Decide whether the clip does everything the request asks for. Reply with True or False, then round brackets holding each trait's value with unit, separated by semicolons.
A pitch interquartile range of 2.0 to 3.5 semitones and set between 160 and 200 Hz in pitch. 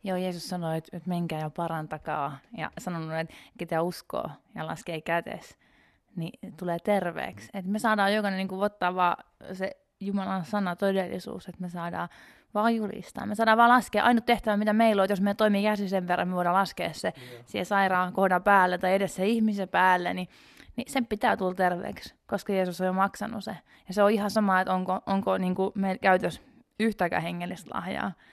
True (2.7 semitones; 190 Hz)